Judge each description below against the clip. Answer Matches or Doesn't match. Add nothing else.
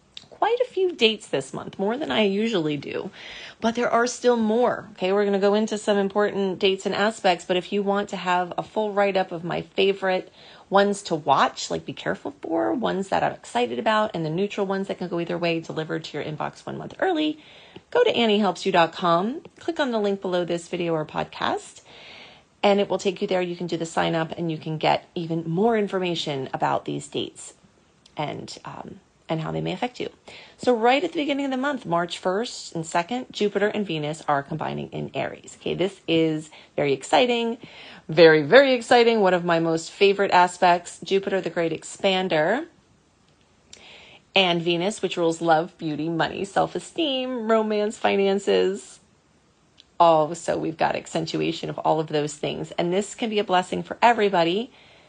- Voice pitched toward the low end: Doesn't match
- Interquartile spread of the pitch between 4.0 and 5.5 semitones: Matches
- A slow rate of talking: Doesn't match